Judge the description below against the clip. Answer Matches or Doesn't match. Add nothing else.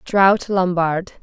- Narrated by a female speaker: Matches